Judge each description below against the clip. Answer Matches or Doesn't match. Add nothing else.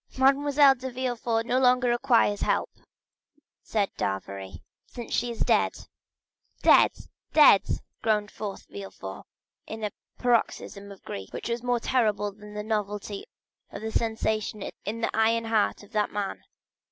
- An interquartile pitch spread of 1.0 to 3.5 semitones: Matches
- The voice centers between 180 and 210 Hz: Doesn't match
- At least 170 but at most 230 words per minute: Doesn't match